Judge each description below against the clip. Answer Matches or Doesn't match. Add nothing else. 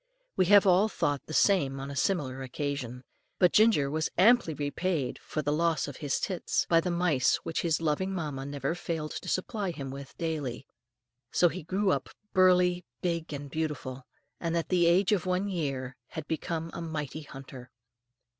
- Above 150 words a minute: Matches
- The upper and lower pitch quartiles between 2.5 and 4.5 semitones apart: Matches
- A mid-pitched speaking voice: Matches